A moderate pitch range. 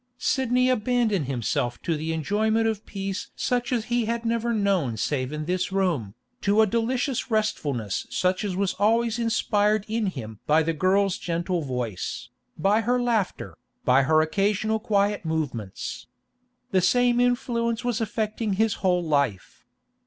No: wide, 6.2 semitones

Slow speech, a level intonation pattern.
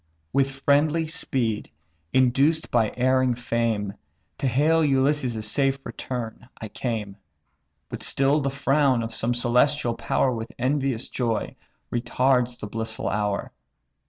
No: slow, 125 wpm; average, 3.1 semitones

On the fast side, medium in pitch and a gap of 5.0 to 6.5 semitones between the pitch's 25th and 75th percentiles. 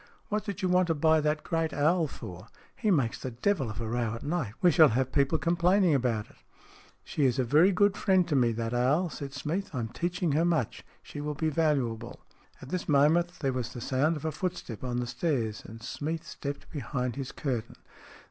Yes: fast, 225 wpm; medium, 145 Hz; wide, 5.5 semitones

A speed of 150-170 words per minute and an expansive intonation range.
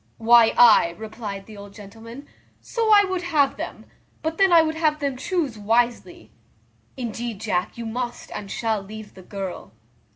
Yes: average, 165 wpm; wide, 6.2 semitones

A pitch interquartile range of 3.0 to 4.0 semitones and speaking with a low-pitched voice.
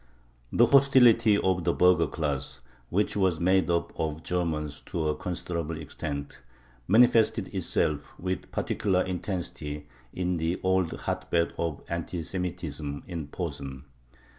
Yes: average, 3.5 semitones; very low, 85 Hz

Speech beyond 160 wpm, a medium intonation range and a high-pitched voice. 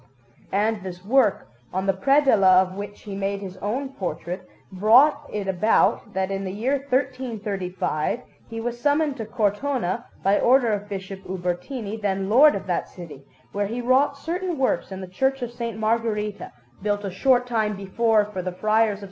Yes: average, 180 wpm; average, 4.3 semitones; high, 210 Hz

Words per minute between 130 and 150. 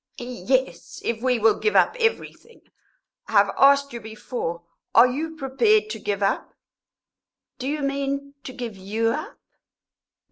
Yes: average, 145 wpm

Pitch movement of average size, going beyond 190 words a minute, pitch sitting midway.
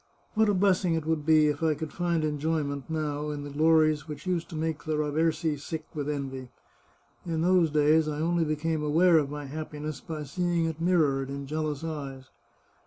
No: narrow, 1.8 semitones; average, 200 wpm; medium, 155 Hz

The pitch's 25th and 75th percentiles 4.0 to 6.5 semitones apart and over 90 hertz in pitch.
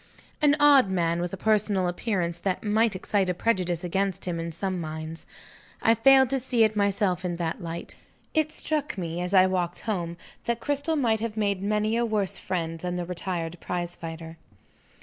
Yes: average, 4.3 semitones; high, 190 Hz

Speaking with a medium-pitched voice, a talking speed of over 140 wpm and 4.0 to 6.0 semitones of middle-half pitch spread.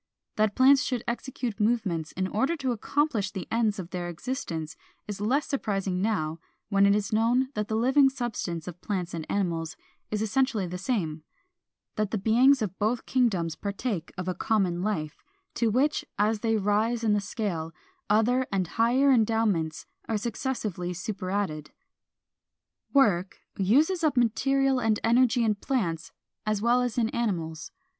No: high, 215 Hz; average, 160 wpm; average, 4.6 semitones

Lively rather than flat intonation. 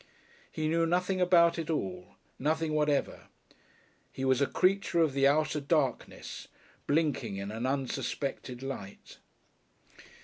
No: average, 3.9 semitones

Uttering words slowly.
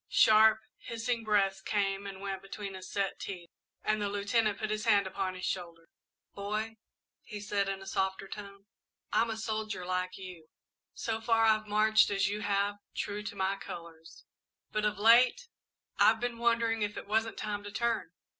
No: average, 175 wpm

